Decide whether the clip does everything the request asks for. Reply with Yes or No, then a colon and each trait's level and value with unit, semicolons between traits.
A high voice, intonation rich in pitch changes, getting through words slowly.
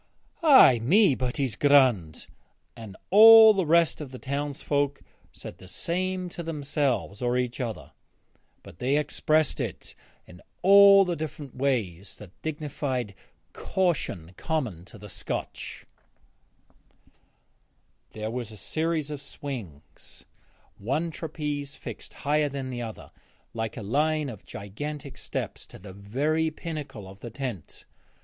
No: medium, 140 Hz; wide, 5.7 semitones; slow, 130 wpm